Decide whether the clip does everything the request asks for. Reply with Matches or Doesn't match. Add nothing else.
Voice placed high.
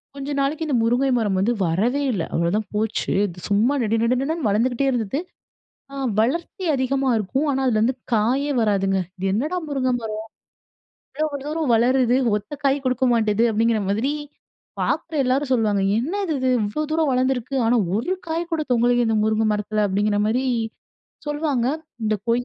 Matches